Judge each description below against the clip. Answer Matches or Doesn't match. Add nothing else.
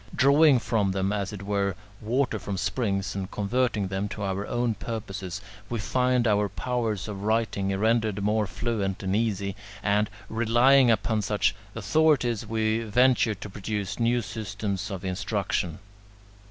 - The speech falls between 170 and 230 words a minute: Doesn't match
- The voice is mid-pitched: Doesn't match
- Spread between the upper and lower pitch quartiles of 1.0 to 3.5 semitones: Matches